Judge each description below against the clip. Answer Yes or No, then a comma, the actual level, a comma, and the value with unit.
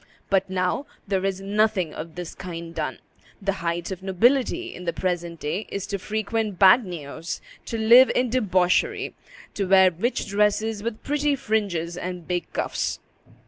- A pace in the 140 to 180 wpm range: Yes, average, 155 wpm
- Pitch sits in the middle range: No, high, 195 Hz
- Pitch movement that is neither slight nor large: Yes, average, 3.6 semitones